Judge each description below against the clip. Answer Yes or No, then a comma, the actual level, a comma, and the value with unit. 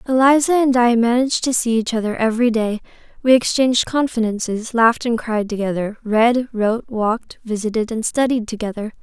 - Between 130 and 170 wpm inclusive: Yes, average, 160 wpm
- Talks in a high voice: Yes, high, 230 Hz